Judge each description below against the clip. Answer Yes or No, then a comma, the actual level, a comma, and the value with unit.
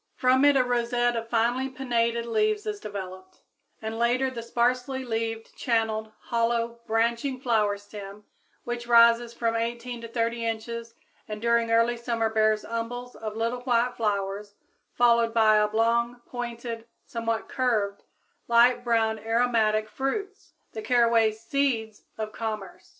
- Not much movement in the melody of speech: Yes, narrow, 1.6 semitones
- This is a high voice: Yes, high, 230 Hz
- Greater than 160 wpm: No, slow, 135 wpm